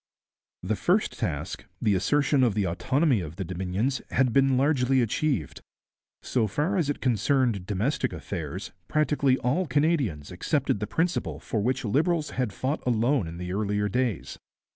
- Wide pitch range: Yes, wide, 6.3 semitones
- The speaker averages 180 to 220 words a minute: No, average, 155 wpm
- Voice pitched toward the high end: No, low, 125 Hz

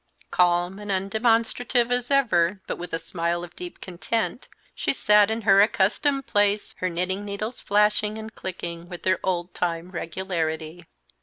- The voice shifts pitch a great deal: No, average, 3.7 semitones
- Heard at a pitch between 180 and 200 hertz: Yes, high, 190 Hz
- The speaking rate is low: No, average, 155 wpm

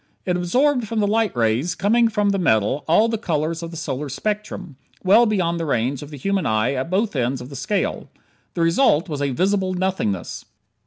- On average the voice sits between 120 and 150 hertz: No, medium, 170 Hz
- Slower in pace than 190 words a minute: No, fast, 205 wpm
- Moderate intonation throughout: No, wide, 6.6 semitones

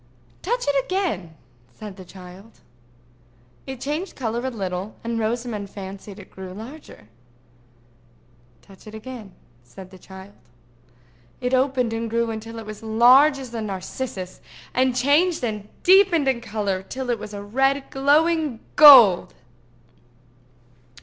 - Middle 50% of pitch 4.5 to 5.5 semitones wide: Yes, average, 5.0 semitones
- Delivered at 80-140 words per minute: Yes, slow, 135 wpm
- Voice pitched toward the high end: Yes, high, 230 Hz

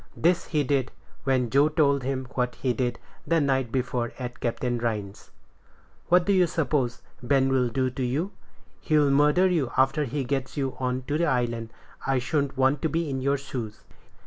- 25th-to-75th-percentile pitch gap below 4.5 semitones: Yes, average, 2.9 semitones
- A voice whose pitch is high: No, low, 135 Hz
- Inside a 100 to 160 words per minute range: No, average, 180 wpm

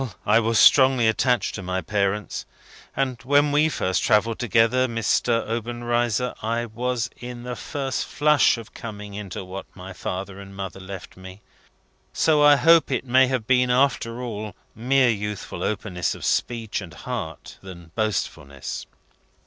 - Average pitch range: Yes, average, 4.1 semitones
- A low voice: Yes, low, 115 Hz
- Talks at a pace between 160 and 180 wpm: No, average, 150 wpm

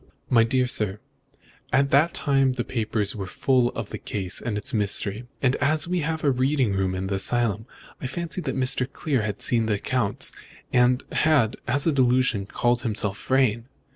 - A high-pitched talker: No, low, 125 Hz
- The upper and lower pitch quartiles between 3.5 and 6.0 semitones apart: Yes, average, 4.3 semitones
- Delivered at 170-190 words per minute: Yes, average, 180 wpm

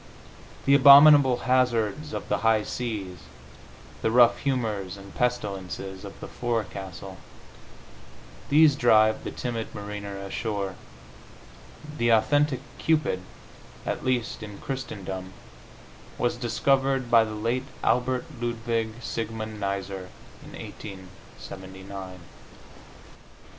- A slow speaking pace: Yes, slow, 100 wpm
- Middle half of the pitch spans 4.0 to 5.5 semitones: Yes, average, 4.3 semitones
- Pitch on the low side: Yes, low, 110 Hz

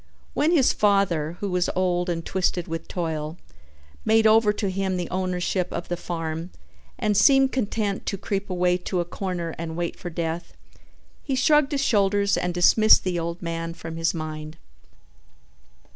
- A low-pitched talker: No, medium, 180 Hz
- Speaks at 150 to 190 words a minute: Yes, average, 165 wpm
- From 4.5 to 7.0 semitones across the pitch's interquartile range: No, average, 3.3 semitones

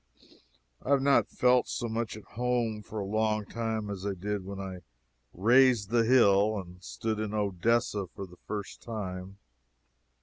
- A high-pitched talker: No, low, 105 Hz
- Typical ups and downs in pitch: Yes, average, 3.0 semitones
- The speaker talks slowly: No, average, 165 wpm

